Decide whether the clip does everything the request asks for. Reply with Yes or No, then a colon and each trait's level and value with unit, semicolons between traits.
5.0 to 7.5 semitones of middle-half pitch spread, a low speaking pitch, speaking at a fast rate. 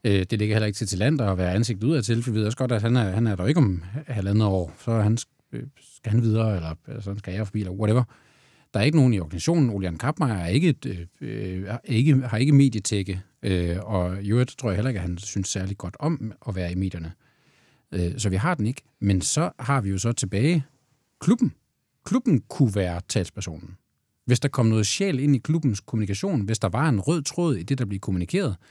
Yes: wide, 5.5 semitones; low, 110 Hz; fast, 230 wpm